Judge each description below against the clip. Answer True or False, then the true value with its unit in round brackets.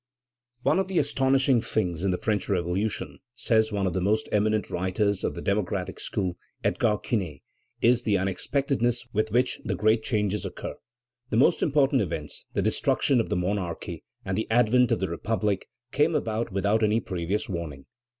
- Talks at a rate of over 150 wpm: True (170 wpm)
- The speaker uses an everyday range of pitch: True (3.9 semitones)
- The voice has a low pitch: True (105 Hz)